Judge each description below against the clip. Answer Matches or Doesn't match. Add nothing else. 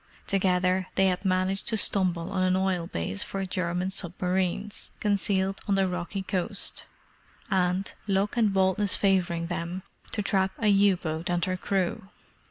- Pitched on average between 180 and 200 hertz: Matches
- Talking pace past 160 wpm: Doesn't match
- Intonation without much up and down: Matches